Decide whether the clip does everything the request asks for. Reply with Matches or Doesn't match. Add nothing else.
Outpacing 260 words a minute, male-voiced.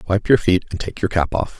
Matches